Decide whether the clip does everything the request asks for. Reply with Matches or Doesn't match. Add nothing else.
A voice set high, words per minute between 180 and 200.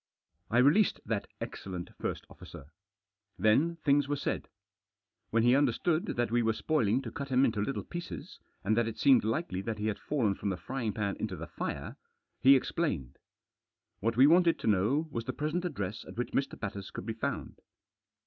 Doesn't match